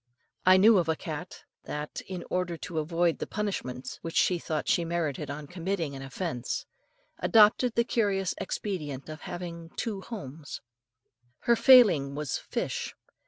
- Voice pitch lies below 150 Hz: No, medium, 170 Hz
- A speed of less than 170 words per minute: Yes, average, 150 wpm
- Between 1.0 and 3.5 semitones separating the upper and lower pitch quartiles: No, average, 4.4 semitones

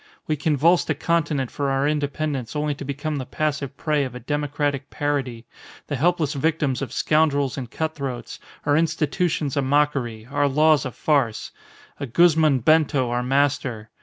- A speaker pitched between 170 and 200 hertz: No, medium, 145 Hz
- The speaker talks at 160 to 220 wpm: Yes, average, 165 wpm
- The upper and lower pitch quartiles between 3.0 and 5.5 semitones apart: No, narrow, 2.5 semitones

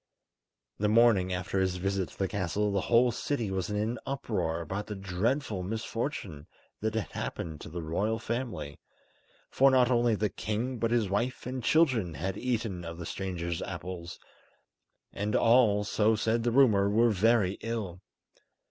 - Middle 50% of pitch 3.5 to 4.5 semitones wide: Yes, average, 4.1 semitones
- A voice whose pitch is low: Yes, low, 105 Hz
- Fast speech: No, average, 165 wpm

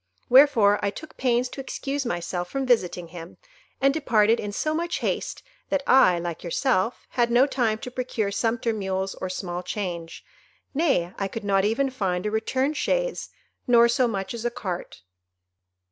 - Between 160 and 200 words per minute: Yes, average, 165 wpm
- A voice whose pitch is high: Yes, high, 225 Hz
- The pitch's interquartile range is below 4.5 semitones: No, wide, 5.6 semitones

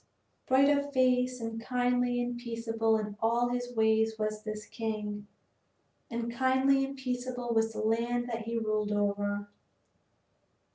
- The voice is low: No, high, 230 Hz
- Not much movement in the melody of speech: Yes, narrow, 2.2 semitones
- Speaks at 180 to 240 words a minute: No, average, 140 wpm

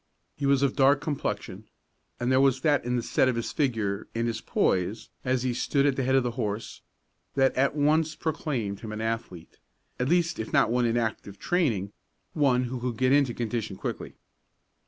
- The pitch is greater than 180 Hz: No, low, 125 Hz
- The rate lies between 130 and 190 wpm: No, average, 200 wpm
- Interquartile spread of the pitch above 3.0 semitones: Yes, average, 3.7 semitones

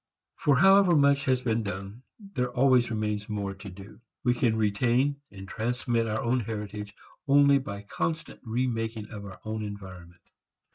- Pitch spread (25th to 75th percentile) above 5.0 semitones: No, average, 3.8 semitones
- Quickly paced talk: No, average, 155 wpm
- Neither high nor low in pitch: No, low, 115 Hz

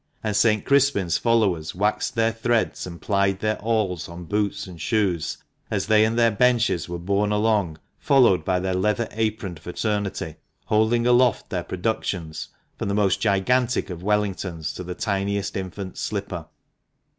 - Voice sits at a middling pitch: No, low, 100 Hz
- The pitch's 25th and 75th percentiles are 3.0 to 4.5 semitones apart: Yes, average, 3.4 semitones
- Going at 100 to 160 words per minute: Yes, average, 155 wpm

